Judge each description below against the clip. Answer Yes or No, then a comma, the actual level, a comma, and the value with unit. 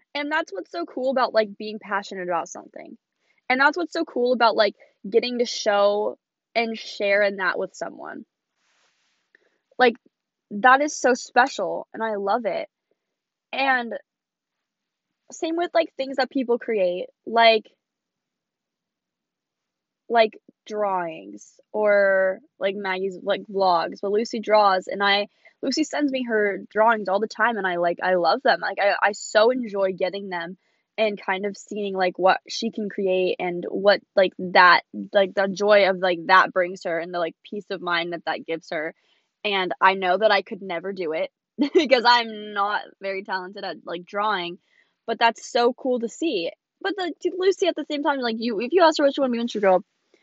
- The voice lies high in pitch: Yes, high, 210 Hz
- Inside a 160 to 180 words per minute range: Yes, average, 175 wpm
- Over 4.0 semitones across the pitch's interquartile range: Yes, average, 4.8 semitones